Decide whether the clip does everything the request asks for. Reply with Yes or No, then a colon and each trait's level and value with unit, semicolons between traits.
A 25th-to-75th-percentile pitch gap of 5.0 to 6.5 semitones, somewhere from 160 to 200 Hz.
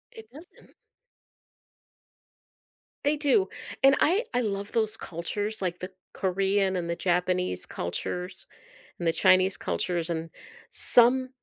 Yes: wide, 5.5 semitones; high, 190 Hz